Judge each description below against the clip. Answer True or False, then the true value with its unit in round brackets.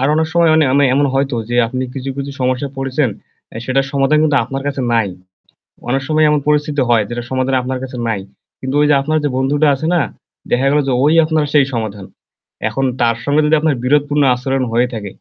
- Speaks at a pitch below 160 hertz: True (135 Hz)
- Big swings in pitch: False (2.6 semitones)